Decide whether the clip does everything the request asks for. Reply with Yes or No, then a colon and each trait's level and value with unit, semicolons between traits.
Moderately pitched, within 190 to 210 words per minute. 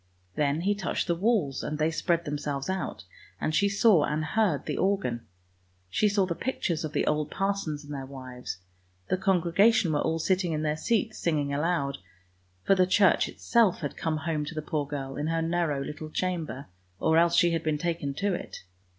Yes: medium, 160 Hz; average, 200 wpm